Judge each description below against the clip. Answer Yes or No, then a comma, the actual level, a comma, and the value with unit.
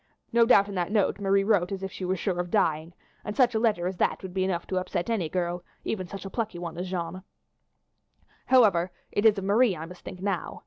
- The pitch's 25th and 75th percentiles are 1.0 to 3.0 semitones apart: Yes, narrow, 2.6 semitones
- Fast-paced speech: Yes, fast, 240 wpm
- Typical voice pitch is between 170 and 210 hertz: Yes, high, 190 Hz